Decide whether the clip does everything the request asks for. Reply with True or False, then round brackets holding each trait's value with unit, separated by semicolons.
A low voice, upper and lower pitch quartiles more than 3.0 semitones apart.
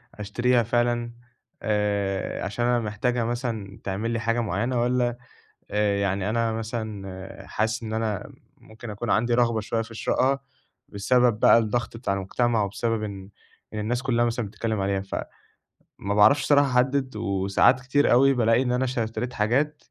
False (115 Hz; 2.7 semitones)